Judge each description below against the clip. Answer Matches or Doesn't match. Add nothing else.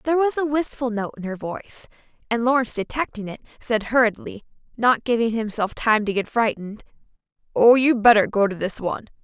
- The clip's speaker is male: Doesn't match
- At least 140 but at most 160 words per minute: Doesn't match